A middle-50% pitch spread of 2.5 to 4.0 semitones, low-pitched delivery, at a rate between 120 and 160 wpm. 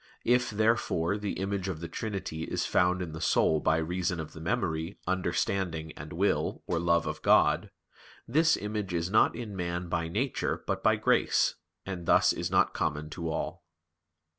No: average, 3.7 semitones; very low, 90 Hz; average, 175 wpm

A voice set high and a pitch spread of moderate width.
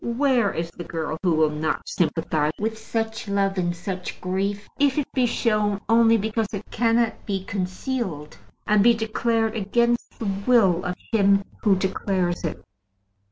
Yes: high, 200 Hz; average, 3.8 semitones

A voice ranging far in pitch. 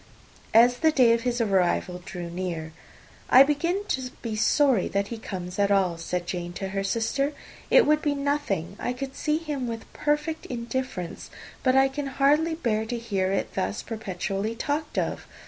Yes: wide, 6.4 semitones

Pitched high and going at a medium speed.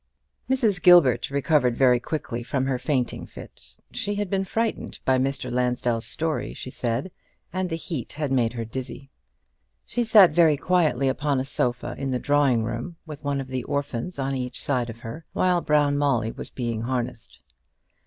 No: low, 135 Hz; average, 175 wpm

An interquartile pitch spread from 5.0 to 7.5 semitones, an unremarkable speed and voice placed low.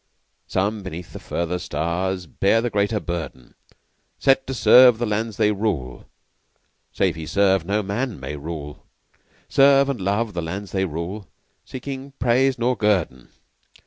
Yes: average, 5.3 semitones; average, 145 wpm; low, 100 Hz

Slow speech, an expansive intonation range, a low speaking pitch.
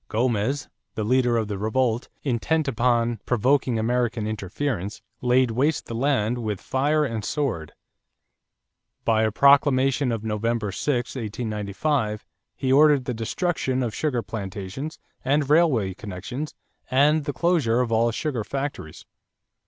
No: slow, 130 wpm; average, 4.1 semitones; low, 120 Hz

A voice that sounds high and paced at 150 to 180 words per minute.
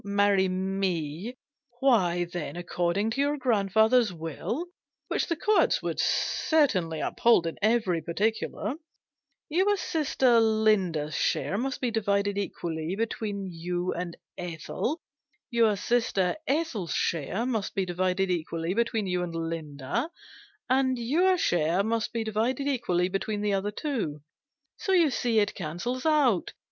No: high, 205 Hz; slow, 135 wpm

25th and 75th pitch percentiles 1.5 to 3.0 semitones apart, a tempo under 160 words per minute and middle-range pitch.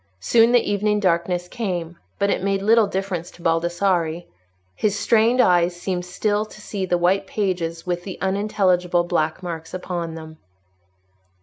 Yes: average, 2.7 semitones; average, 150 wpm; medium, 180 Hz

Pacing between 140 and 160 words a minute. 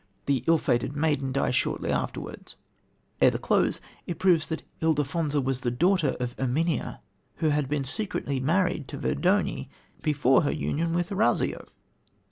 Yes: average, 150 wpm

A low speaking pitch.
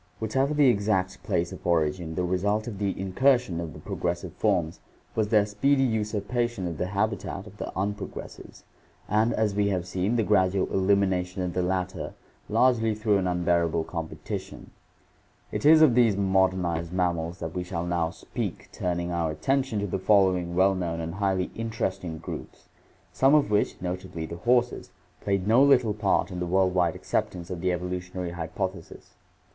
Yes: very low, 95 Hz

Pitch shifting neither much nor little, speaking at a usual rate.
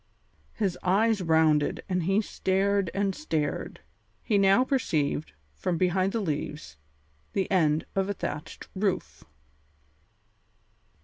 No: average, 4.0 semitones; slow, 115 wpm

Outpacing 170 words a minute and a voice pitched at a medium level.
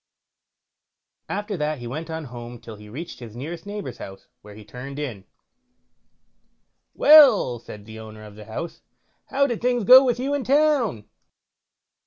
No: average, 160 wpm; medium, 150 Hz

